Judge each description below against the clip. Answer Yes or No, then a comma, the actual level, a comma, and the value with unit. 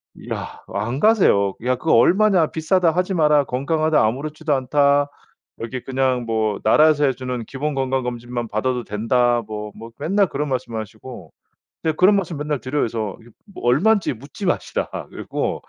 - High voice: No, low, 135 Hz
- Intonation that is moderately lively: Yes, average, 4.7 semitones